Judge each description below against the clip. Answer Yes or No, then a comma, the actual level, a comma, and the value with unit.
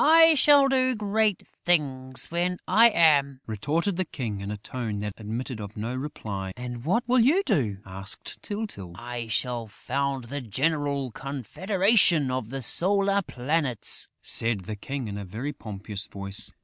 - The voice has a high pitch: No, low, 135 Hz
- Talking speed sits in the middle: Yes, average, 160 wpm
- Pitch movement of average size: No, wide, 8.7 semitones